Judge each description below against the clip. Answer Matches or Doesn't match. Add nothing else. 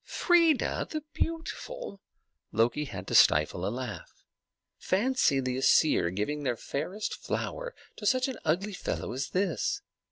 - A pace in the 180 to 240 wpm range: Doesn't match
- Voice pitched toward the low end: Doesn't match